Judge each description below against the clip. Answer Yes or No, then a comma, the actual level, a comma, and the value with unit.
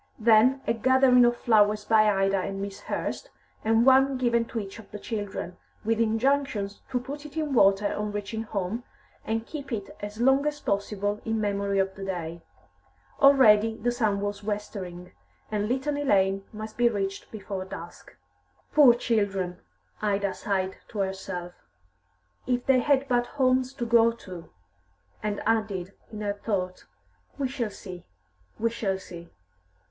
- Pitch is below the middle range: No, high, 215 Hz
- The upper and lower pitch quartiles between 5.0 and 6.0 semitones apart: No, average, 3.5 semitones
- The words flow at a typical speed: Yes, average, 155 wpm